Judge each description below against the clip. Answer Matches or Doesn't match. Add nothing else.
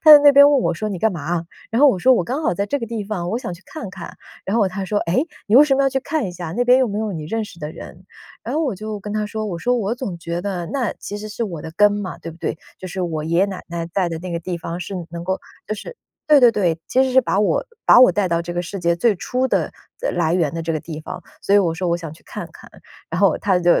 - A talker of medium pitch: Doesn't match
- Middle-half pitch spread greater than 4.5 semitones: Matches